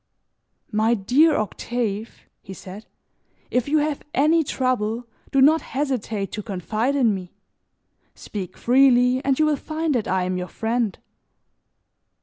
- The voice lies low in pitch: No, high, 245 Hz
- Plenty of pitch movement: No, average, 4.7 semitones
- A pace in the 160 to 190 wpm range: No, slow, 135 wpm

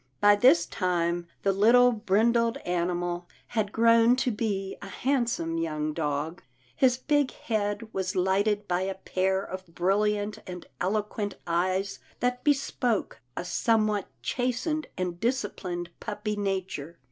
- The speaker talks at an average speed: No, slow, 130 wpm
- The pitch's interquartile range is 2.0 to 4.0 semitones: No, average, 4.4 semitones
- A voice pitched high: Yes, high, 200 Hz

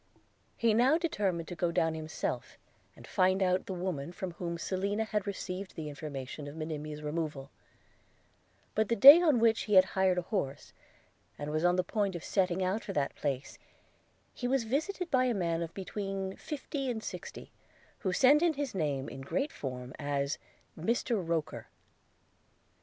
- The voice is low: No, medium, 185 Hz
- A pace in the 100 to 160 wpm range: No, average, 175 wpm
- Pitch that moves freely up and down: Yes, wide, 6.0 semitones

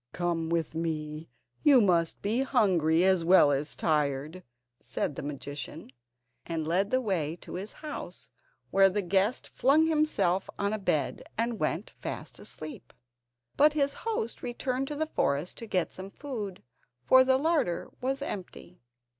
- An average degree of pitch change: No, wide, 7.9 semitones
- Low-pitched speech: No, high, 190 Hz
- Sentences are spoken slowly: No, average, 155 wpm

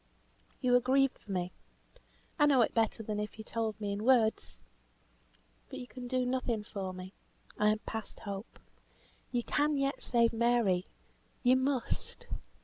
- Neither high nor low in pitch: No, high, 230 Hz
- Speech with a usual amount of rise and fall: Yes, average, 3.3 semitones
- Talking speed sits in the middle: Yes, average, 160 wpm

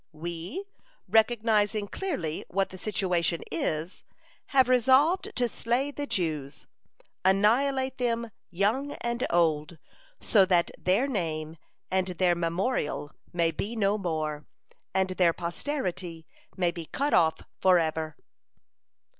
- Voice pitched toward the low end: No, high, 190 Hz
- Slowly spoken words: Yes, slow, 115 wpm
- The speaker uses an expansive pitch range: Yes, wide, 6.1 semitones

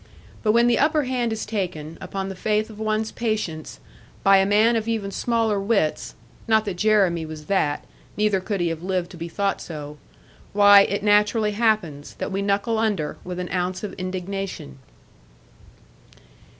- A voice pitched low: No, high, 200 Hz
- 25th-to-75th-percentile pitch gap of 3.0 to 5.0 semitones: Yes, average, 3.3 semitones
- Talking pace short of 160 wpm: No, average, 170 wpm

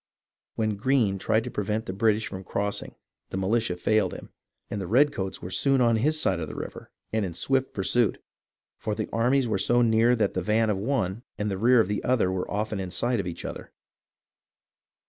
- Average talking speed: No, fast, 210 wpm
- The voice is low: Yes, low, 110 Hz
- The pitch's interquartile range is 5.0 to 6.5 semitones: No, average, 3.7 semitones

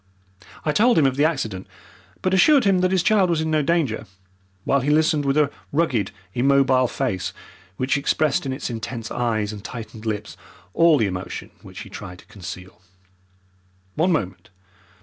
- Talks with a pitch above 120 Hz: Yes, low, 135 Hz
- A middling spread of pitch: No, wide, 6.4 semitones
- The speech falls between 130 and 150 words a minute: No, average, 170 wpm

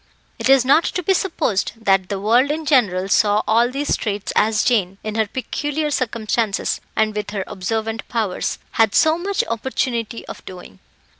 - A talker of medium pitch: No, high, 225 Hz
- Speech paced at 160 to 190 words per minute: Yes, average, 170 wpm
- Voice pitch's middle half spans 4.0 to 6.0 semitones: Yes, average, 4.3 semitones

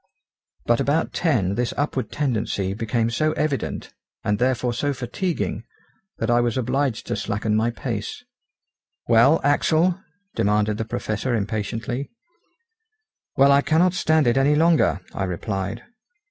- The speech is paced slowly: Yes, slow, 130 wpm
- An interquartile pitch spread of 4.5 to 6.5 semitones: Yes, average, 4.9 semitones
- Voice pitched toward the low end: Yes, low, 120 Hz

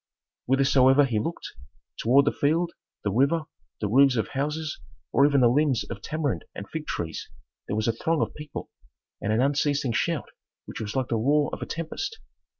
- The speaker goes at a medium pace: Yes, average, 185 wpm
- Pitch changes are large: No, average, 4.3 semitones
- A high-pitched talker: No, medium, 140 Hz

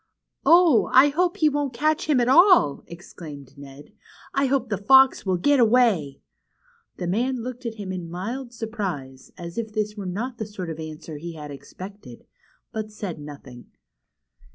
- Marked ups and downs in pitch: Yes, wide, 7.6 semitones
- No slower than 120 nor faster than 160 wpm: No, average, 175 wpm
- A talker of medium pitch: No, high, 210 Hz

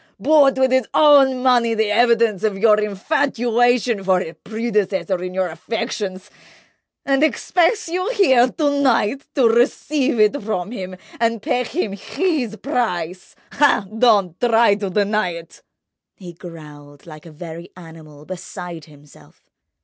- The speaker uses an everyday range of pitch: No, wide, 5.7 semitones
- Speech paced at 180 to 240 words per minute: No, slow, 135 wpm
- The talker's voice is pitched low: No, high, 220 Hz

